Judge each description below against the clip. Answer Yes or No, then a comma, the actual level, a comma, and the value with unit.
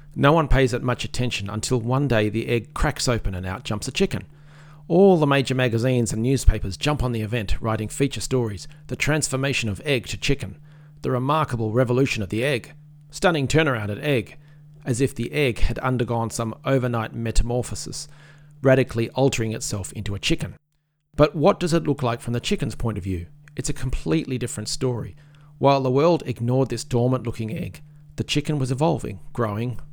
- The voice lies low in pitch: Yes, low, 130 Hz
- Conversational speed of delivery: Yes, average, 185 wpm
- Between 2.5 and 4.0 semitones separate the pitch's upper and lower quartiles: No, average, 4.5 semitones